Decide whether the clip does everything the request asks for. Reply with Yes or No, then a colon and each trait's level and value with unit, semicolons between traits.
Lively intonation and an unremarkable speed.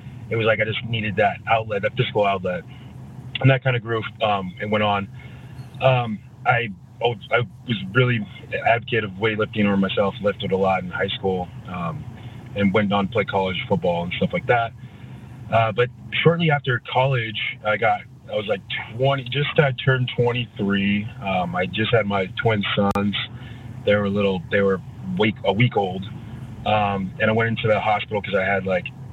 No: average, 3.8 semitones; average, 185 wpm